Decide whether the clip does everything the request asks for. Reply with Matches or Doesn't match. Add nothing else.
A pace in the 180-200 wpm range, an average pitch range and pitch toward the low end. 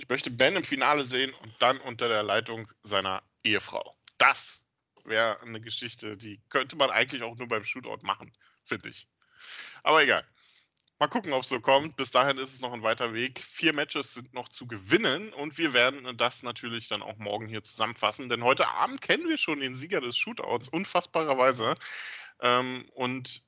Matches